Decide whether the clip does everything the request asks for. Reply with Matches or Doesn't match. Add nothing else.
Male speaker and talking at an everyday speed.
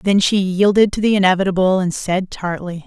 Doesn't match